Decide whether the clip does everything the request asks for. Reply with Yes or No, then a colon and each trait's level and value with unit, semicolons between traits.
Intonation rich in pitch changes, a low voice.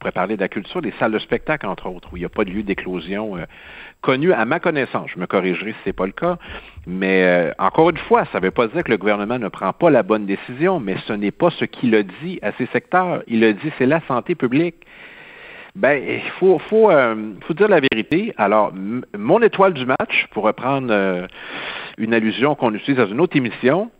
Yes: wide, 8.8 semitones; low, 125 Hz